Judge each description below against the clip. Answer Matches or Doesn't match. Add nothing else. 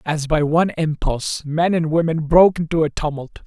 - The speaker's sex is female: Doesn't match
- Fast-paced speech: Doesn't match